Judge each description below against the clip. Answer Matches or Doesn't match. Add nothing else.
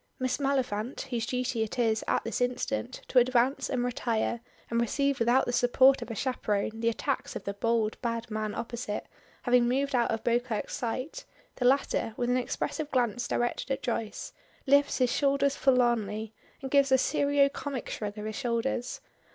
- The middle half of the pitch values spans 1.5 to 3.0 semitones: Matches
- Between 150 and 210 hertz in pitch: Doesn't match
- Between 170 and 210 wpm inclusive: Matches